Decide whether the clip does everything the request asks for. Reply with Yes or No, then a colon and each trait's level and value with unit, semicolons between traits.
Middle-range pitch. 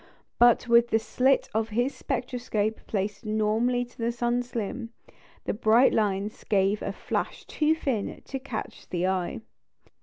No: high, 230 Hz